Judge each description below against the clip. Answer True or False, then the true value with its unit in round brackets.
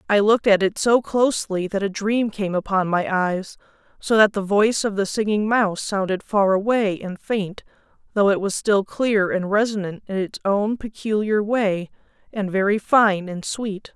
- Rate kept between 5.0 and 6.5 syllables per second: False (4.6 syllables/s)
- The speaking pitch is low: False (205 Hz)